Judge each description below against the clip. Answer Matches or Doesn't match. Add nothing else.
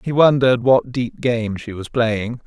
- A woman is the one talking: Doesn't match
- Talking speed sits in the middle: Matches